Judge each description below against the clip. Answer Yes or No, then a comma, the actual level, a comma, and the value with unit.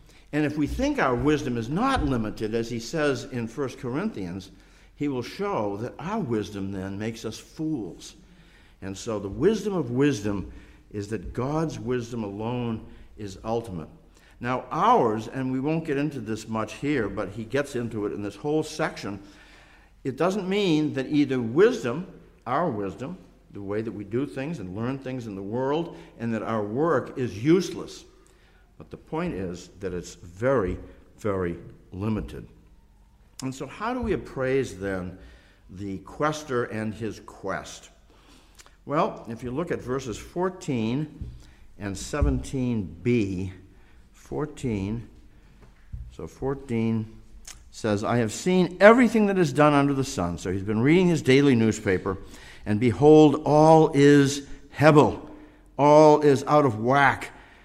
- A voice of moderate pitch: No, low, 120 Hz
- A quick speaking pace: No, average, 150 wpm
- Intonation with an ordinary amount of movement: No, wide, 6.2 semitones